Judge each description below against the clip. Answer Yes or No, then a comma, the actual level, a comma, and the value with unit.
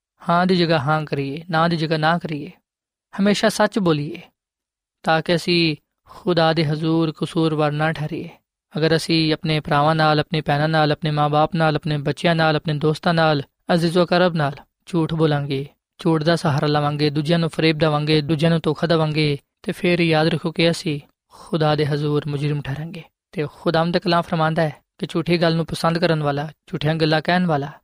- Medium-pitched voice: Yes, medium, 160 Hz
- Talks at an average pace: No, fast, 175 wpm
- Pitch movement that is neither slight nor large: No, narrow, 1.8 semitones